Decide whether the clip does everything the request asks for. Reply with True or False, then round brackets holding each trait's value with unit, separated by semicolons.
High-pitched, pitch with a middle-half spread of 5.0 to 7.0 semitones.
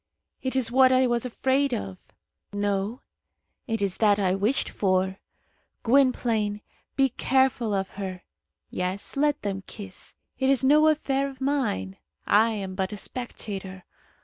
True (225 Hz; 5.3 semitones)